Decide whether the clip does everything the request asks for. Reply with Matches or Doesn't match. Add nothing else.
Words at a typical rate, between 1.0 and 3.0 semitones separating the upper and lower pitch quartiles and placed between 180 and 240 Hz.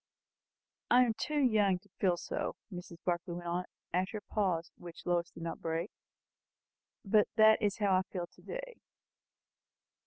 Doesn't match